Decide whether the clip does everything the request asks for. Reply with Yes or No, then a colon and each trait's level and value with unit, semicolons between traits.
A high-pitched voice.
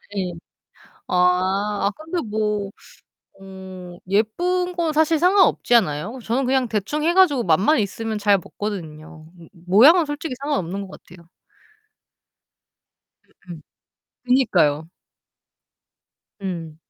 Yes: high, 205 Hz